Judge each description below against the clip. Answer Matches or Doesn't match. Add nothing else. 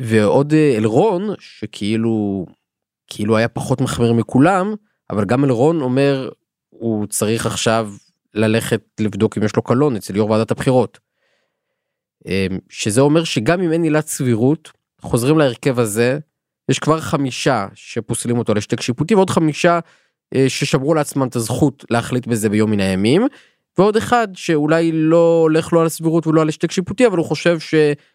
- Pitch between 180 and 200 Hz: Doesn't match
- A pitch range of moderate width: Doesn't match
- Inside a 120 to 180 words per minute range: Matches